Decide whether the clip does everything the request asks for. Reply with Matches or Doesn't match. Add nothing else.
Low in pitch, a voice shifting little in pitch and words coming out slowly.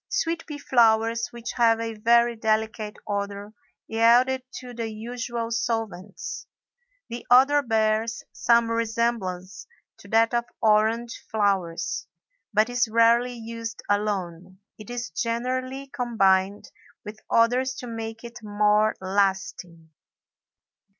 Doesn't match